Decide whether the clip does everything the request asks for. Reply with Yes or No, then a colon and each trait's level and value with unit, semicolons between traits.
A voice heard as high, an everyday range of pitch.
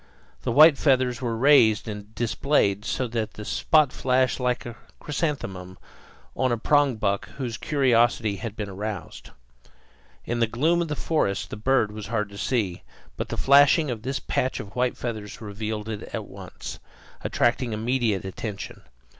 No: low, 115 Hz; average, 3.9 semitones